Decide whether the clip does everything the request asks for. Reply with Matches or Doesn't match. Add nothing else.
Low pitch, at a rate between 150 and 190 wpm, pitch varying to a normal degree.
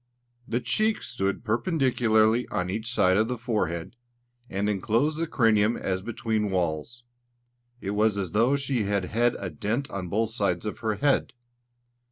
Matches